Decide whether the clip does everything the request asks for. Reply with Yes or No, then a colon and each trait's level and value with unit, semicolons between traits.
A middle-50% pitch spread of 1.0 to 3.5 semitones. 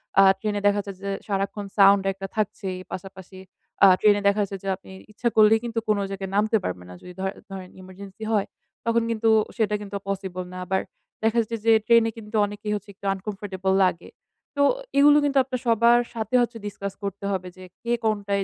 Yes: narrow, 2.4 semitones